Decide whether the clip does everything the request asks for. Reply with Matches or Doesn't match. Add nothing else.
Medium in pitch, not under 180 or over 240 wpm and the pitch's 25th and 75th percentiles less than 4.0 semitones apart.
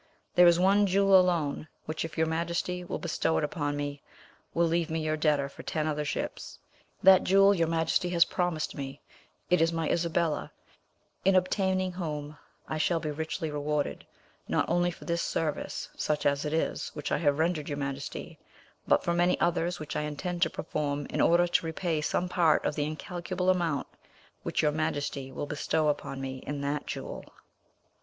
Matches